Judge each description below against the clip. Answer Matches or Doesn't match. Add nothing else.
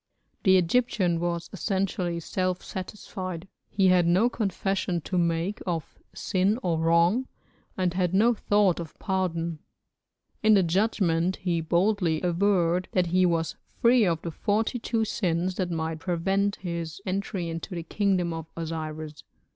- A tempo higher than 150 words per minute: Doesn't match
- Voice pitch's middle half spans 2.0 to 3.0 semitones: Matches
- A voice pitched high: Doesn't match